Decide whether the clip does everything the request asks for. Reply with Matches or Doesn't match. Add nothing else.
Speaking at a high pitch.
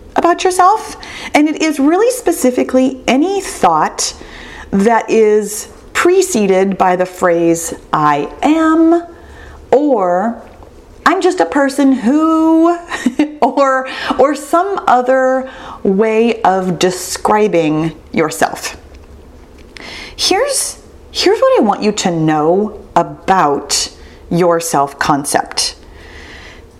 Matches